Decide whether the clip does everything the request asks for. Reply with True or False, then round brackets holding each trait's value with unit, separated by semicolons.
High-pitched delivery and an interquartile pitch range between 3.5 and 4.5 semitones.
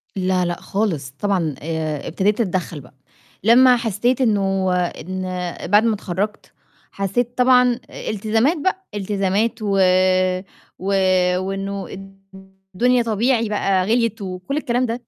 True (205 Hz; 3.8 semitones)